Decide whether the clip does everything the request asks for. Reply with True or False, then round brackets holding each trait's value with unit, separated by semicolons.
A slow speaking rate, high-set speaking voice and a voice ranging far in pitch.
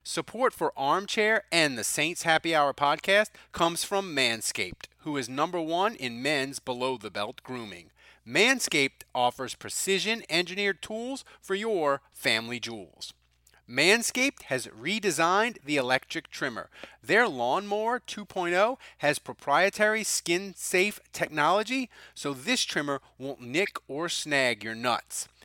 False (120 wpm; 160 Hz; 7.6 semitones)